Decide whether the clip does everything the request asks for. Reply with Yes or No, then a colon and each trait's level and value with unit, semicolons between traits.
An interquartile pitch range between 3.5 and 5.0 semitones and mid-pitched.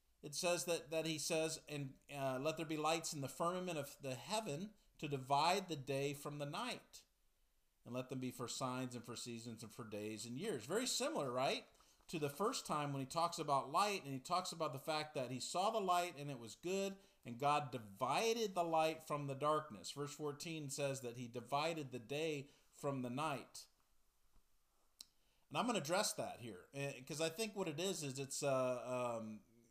Yes: average, 4.0 semitones; medium, 145 Hz